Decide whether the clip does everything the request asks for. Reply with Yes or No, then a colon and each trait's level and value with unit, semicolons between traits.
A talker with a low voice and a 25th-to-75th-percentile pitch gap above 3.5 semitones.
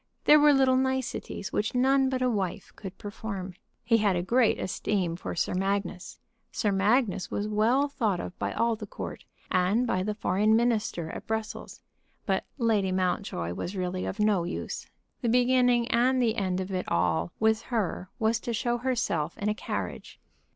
No: high, 210 Hz; average, 4.4 semitones